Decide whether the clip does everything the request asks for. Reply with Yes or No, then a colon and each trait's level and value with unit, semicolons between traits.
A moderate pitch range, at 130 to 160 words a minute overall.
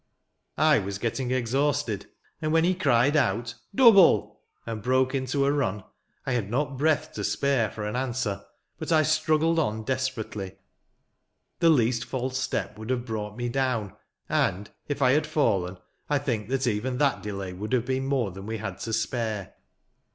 No: average, 4.6 semitones; average, 180 wpm